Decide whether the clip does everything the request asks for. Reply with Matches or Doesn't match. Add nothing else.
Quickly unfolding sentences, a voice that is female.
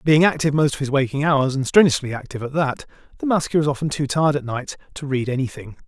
Doesn't match